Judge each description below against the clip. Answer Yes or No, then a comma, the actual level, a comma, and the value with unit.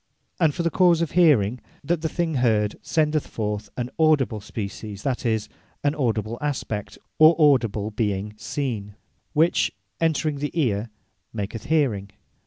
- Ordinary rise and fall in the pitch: No, wide, 6.7 semitones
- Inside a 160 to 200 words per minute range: No, average, 150 wpm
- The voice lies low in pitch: Yes, low, 125 Hz